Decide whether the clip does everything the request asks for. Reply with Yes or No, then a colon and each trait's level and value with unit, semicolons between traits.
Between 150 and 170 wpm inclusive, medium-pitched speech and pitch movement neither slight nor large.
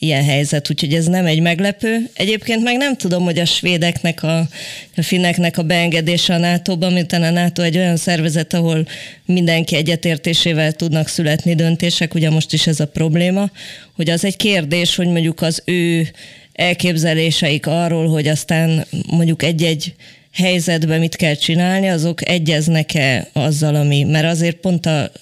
No: fast, 155 wpm; medium, 170 Hz; narrow, 1.6 semitones